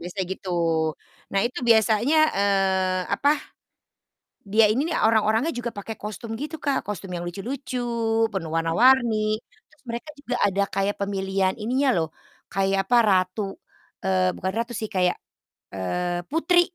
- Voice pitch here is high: Yes, high, 210 Hz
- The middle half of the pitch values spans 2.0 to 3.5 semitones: No, average, 4.3 semitones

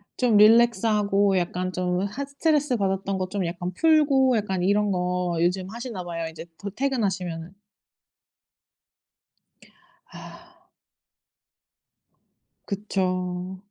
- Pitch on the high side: Yes, high, 195 Hz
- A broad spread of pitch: No, average, 3.9 semitones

